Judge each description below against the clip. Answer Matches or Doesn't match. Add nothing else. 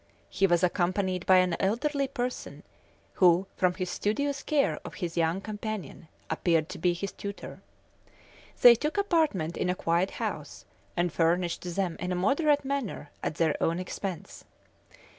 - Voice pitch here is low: Doesn't match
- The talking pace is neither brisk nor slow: Matches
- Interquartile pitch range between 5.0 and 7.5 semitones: Matches